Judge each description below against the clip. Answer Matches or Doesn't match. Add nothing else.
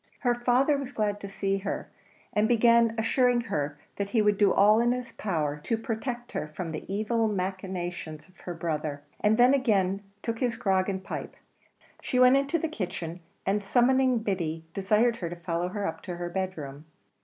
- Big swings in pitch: Doesn't match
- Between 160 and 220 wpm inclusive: Matches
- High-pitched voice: Matches